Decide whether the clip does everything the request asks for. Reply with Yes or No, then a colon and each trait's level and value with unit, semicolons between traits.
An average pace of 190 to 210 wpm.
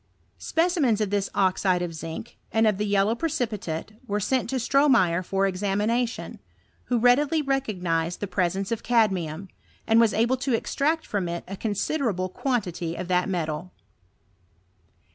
No: average, 150 wpm